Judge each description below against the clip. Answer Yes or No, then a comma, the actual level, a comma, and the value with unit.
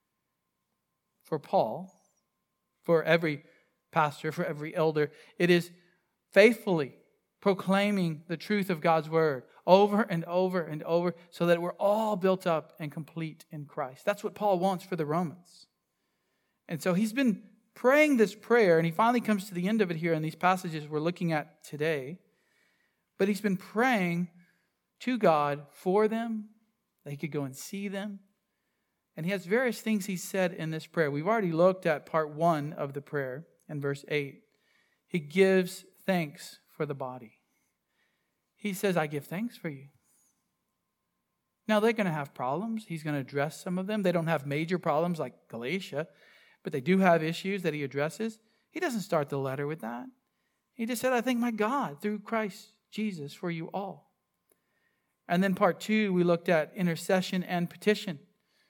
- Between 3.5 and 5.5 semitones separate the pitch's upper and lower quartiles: Yes, average, 4.6 semitones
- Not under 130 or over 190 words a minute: Yes, average, 175 wpm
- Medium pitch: Yes, medium, 180 Hz